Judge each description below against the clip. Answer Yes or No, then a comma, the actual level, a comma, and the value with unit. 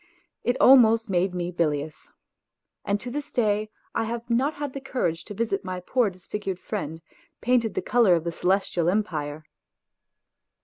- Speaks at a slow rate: No, average, 160 wpm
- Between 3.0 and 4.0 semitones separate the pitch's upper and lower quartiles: No, average, 5.3 semitones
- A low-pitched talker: No, high, 205 Hz